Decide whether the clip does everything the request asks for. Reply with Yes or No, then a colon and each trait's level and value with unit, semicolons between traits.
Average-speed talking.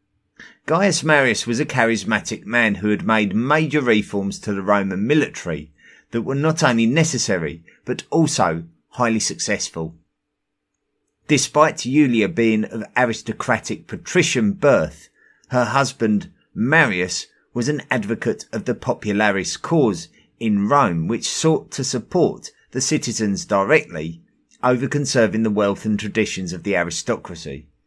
No: slow, 125 wpm